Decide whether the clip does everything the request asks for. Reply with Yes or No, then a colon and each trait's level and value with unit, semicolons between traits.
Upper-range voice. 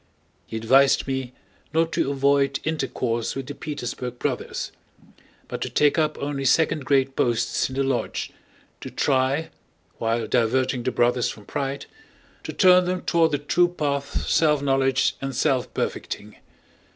No: low, 135 Hz